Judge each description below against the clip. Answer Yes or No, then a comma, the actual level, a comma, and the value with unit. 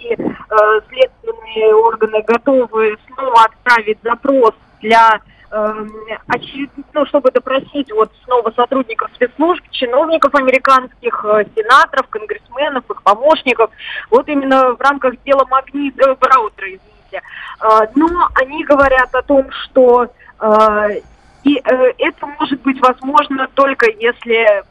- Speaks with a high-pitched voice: Yes, very high, 265 Hz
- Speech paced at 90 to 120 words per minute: Yes, average, 115 wpm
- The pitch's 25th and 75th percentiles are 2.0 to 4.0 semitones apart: No, average, 4.4 semitones